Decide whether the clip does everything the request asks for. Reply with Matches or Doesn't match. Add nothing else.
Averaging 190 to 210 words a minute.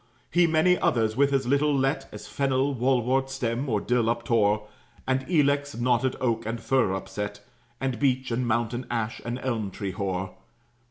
Doesn't match